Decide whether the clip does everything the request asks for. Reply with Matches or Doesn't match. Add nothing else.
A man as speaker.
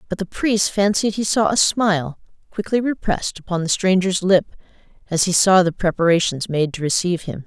Doesn't match